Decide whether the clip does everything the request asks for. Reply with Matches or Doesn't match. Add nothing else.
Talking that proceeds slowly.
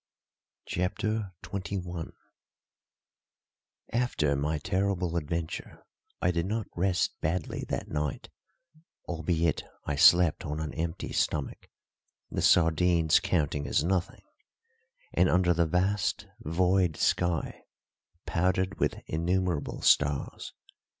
Matches